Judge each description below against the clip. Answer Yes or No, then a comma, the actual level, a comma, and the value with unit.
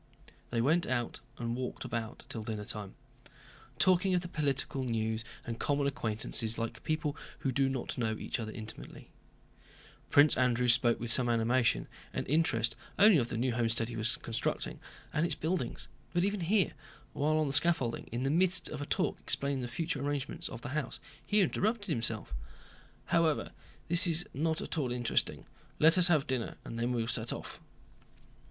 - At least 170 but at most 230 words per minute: Yes, average, 175 wpm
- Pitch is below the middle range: Yes, low, 130 Hz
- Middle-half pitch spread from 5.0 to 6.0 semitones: Yes, wide, 5.4 semitones